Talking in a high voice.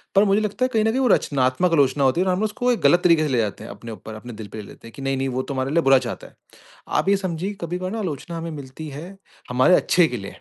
No: medium, 155 Hz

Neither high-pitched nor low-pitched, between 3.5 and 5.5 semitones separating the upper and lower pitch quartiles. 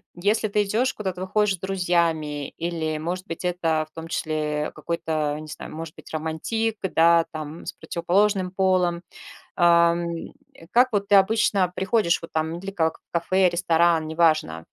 No: medium, 170 Hz; average, 3.1 semitones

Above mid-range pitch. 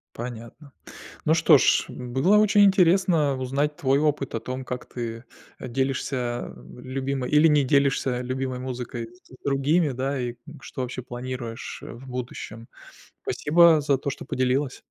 No: low, 130 Hz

